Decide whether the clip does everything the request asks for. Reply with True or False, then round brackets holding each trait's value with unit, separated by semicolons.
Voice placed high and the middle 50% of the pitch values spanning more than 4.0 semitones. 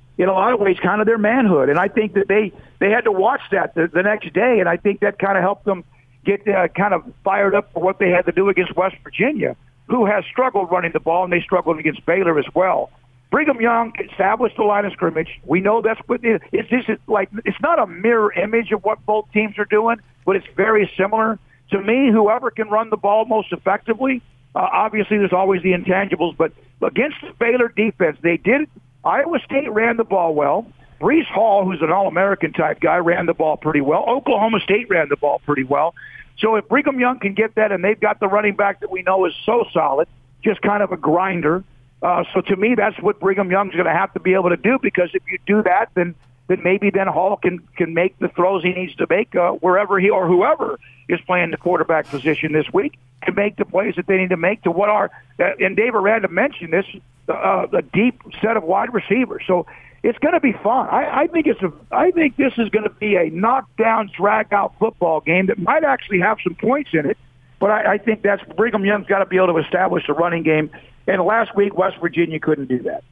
False (195 Hz; 3.6 semitones)